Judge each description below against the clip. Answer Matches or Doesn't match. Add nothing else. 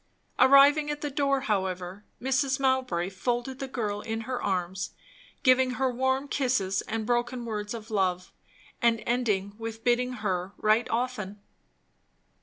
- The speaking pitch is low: Doesn't match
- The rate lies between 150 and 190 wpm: Doesn't match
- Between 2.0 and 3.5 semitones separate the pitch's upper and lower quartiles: Doesn't match